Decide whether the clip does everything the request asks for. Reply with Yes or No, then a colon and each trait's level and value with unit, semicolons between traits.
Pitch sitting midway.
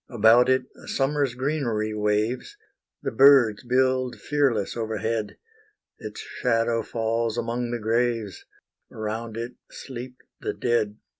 No: low, 120 Hz